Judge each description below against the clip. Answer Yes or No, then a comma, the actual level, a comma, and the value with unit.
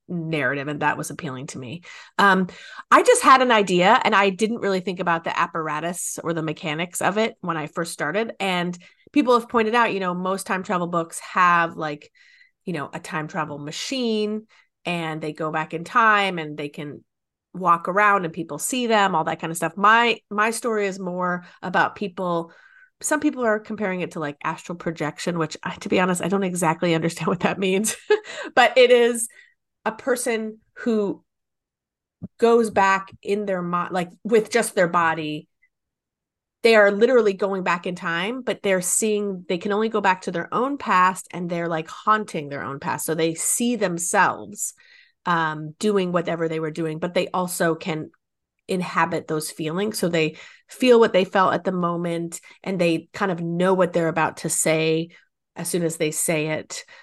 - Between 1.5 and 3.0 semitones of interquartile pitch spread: No, average, 4.5 semitones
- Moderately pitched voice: Yes, medium, 180 Hz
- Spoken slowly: No, average, 190 wpm